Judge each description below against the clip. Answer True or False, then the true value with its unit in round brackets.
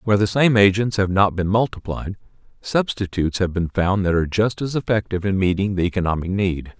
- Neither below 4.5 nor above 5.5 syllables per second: False (5.9 syllables/s)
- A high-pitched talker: False (100 Hz)